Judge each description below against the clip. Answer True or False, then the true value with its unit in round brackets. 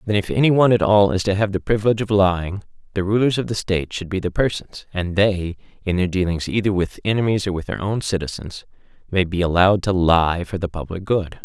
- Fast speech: True (230 wpm)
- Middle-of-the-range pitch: False (95 Hz)